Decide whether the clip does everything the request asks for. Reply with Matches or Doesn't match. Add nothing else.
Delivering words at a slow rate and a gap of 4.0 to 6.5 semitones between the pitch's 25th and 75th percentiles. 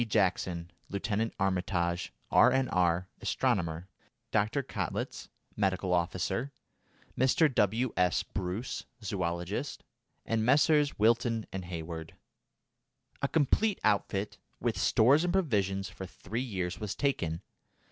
Matches